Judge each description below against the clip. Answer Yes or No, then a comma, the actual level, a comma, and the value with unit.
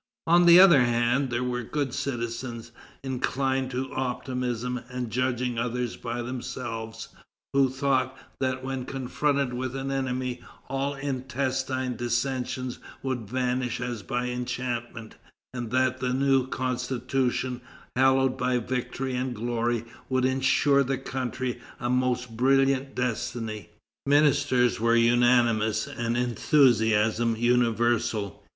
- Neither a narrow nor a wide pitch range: No, narrow, 1.6 semitones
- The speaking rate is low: Yes, slow, 120 wpm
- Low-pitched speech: Yes, low, 125 Hz